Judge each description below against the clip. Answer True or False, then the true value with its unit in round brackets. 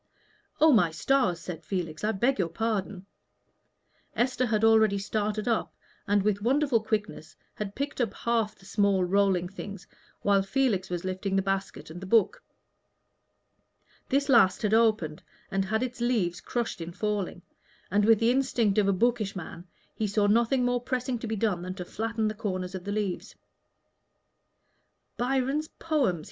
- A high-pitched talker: True (210 Hz)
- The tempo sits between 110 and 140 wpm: False (165 wpm)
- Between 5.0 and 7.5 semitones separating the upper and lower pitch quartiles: False (3.7 semitones)